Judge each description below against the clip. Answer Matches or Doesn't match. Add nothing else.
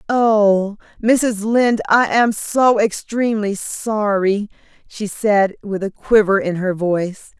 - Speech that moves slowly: Matches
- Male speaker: Doesn't match